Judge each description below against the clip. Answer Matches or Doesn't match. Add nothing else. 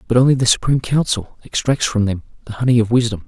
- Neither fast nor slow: Doesn't match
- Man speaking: Matches